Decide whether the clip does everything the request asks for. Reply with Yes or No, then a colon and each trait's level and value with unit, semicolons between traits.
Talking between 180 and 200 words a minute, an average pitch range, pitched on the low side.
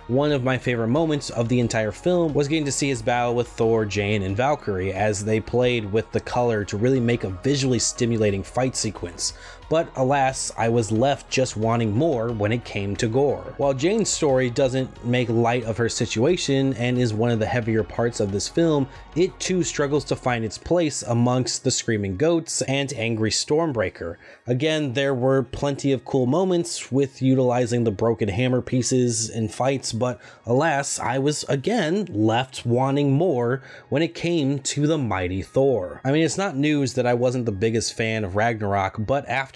Yes: average, 190 wpm; average, 3.5 semitones; low, 125 Hz